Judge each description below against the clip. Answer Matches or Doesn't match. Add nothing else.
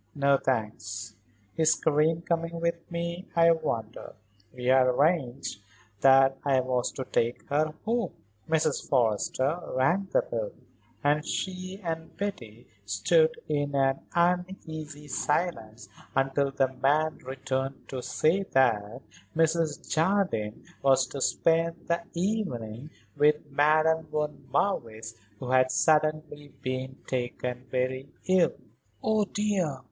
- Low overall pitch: Doesn't match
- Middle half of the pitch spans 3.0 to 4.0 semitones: Doesn't match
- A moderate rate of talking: Doesn't match